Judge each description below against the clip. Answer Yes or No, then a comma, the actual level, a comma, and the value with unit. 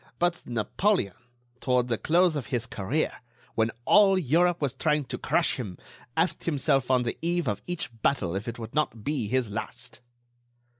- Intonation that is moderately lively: No, wide, 6.5 semitones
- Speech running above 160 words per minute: Yes, average, 170 wpm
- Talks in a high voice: No, low, 130 Hz